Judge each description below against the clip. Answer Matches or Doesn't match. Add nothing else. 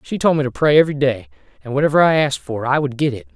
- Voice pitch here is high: Doesn't match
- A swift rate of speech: Matches